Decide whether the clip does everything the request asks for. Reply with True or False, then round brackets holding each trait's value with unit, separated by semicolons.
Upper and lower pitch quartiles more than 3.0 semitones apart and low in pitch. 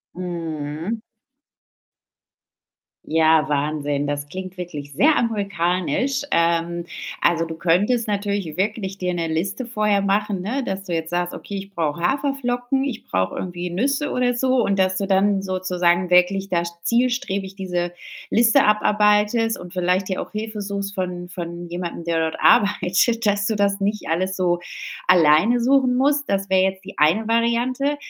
False (4.0 semitones; 190 Hz)